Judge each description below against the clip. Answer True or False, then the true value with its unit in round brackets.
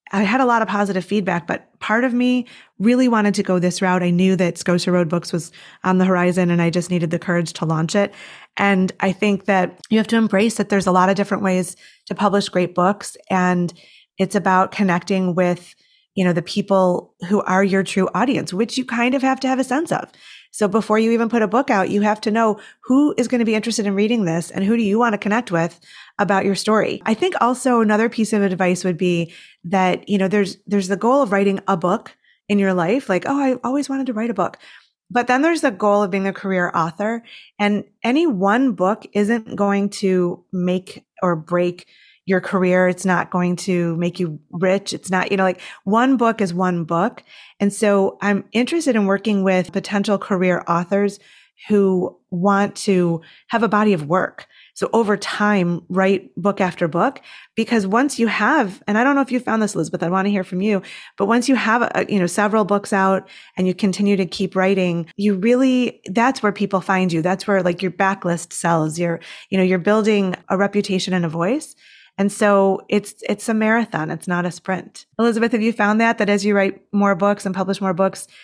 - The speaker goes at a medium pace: False (220 wpm)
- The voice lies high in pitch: True (200 Hz)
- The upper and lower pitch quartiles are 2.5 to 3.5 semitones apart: True (3.1 semitones)